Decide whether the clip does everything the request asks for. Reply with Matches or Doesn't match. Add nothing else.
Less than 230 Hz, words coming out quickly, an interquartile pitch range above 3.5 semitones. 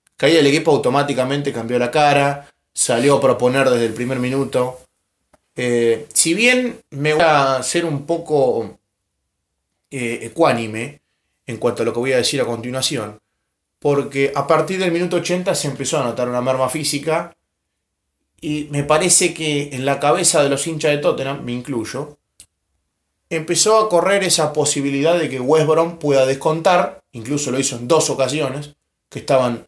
Doesn't match